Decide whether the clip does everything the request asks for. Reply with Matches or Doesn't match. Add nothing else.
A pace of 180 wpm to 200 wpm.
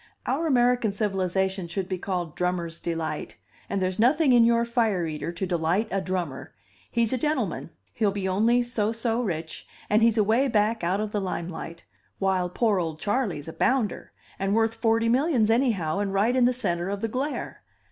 Matches